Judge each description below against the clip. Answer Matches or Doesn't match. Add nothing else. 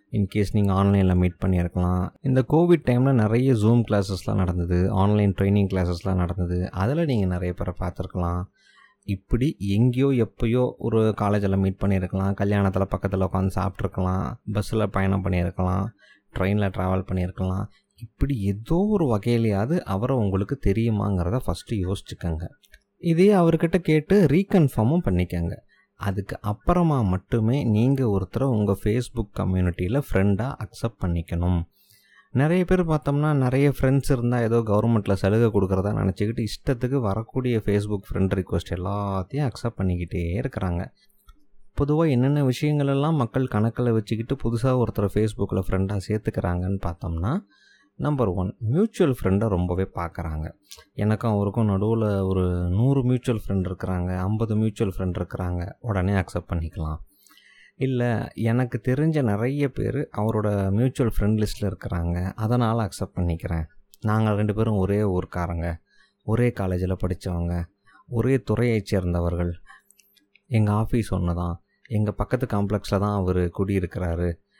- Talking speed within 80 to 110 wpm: Doesn't match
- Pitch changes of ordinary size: Matches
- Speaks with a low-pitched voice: Matches